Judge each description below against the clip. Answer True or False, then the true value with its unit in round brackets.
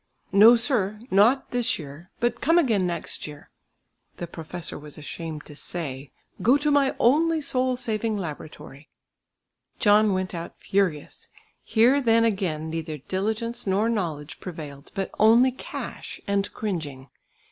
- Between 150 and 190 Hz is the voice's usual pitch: False (200 Hz)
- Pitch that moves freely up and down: True (6.6 semitones)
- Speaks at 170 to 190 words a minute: False (135 wpm)